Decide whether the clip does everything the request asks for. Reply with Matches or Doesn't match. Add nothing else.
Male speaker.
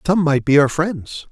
Matches